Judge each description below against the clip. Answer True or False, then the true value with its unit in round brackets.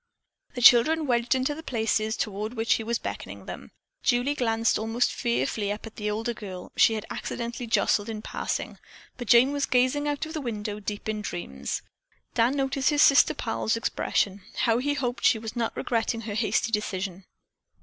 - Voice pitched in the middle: False (230 Hz)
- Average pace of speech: True (180 wpm)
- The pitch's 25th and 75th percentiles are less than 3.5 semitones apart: True (2.9 semitones)